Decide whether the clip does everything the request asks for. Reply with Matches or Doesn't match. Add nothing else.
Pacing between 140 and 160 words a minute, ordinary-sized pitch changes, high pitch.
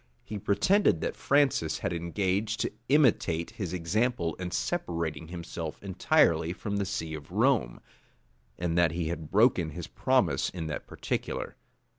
Doesn't match